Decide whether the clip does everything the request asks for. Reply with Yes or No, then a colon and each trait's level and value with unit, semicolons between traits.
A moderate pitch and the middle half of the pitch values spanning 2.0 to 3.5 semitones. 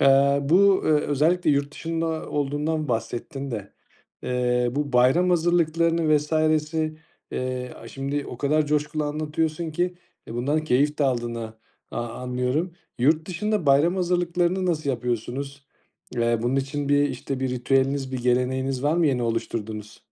No: medium, 145 Hz; average, 3.9 semitones